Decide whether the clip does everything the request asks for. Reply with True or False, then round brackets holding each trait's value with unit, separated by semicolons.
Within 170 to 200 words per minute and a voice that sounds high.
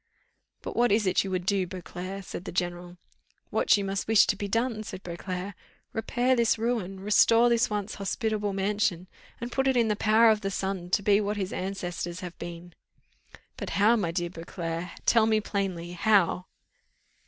True (185 wpm; 195 Hz)